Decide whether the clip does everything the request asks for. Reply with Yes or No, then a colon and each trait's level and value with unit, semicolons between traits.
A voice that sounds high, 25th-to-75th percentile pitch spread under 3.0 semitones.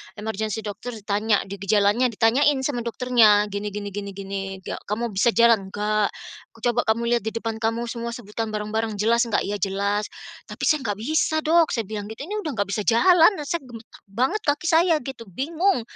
No: high, 225 Hz; average, 3.4 semitones